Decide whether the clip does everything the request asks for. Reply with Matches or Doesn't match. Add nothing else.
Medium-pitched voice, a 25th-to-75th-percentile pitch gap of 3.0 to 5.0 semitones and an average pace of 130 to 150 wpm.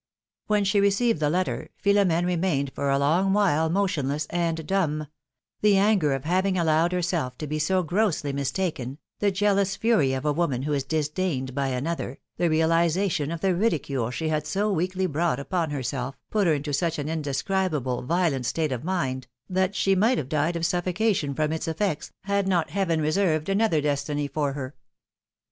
Doesn't match